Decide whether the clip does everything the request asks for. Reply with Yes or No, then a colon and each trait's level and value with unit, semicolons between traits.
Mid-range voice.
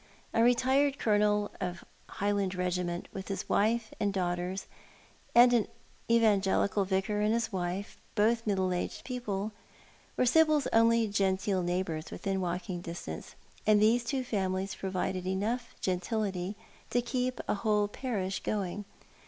No: high, 205 Hz